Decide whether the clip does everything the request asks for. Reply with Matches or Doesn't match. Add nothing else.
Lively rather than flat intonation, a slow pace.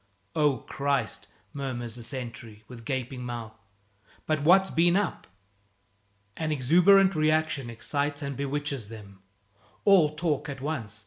Doesn't match